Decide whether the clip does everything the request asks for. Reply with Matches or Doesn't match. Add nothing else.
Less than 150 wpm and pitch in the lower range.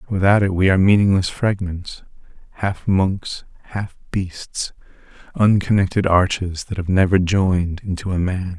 Matches